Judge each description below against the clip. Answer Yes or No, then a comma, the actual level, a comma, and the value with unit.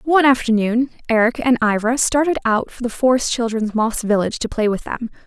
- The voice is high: Yes, high, 235 Hz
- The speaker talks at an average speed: Yes, average, 195 wpm